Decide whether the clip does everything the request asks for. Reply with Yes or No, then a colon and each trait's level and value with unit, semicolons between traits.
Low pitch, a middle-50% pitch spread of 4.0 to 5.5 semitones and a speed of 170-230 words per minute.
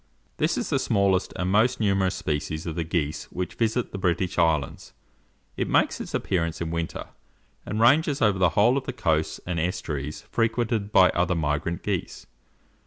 Yes: very low, 90 Hz; average, 4.8 semitones; average, 175 wpm